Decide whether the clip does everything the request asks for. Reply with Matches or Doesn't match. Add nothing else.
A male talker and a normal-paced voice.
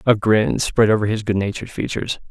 Matches